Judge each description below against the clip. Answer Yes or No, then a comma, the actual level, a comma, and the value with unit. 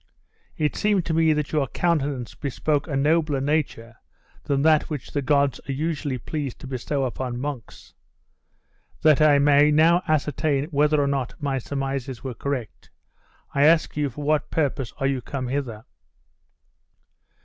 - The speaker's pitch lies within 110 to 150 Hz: Yes, medium, 140 Hz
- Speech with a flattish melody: Yes, narrow, 2.2 semitones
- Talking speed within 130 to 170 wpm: Yes, average, 155 wpm